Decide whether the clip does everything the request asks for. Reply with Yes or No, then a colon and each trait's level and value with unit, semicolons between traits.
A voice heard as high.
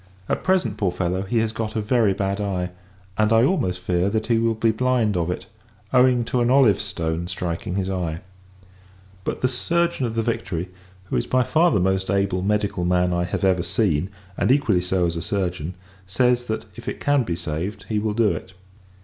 No: low, 100 Hz